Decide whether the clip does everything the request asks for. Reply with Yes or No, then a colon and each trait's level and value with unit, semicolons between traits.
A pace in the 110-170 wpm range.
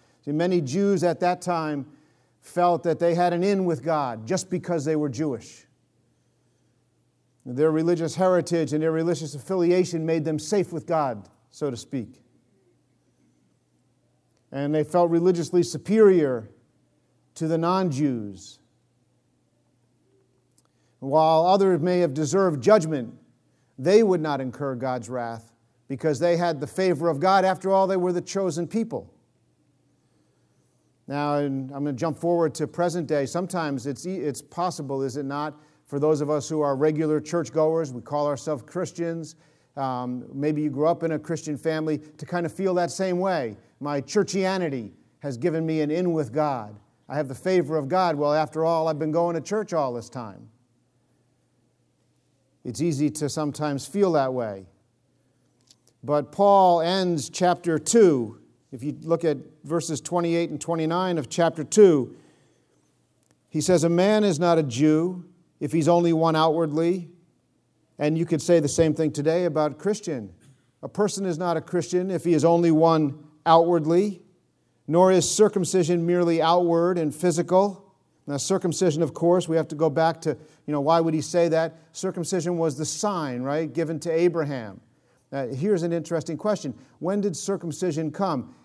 Yes: average, 160 wpm